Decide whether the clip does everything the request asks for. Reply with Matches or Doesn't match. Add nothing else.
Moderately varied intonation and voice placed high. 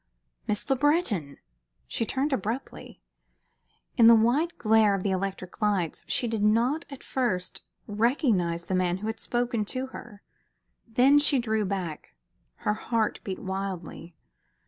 Matches